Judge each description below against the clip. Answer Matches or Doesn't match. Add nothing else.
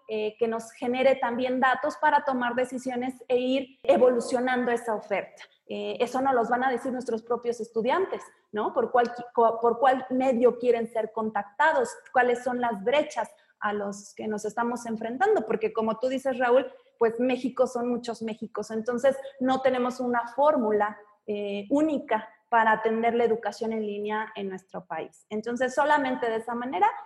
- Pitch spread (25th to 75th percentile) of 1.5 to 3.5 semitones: Matches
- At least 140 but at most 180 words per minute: Matches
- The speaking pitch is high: Matches